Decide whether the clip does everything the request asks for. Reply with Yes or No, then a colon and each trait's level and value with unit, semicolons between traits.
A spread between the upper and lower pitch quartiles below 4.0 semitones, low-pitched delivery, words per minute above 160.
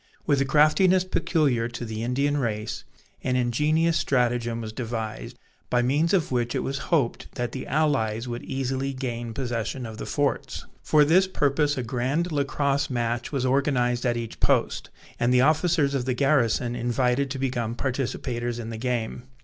Yes: average, 3.1 semitones; low, 130 Hz; average, 170 wpm